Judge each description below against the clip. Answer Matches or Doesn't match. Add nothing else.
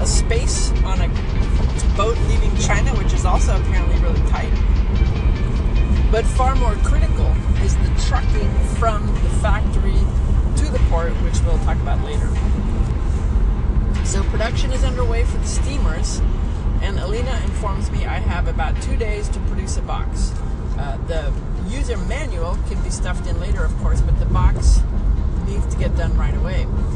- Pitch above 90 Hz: Doesn't match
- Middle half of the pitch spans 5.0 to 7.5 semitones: Doesn't match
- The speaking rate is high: Doesn't match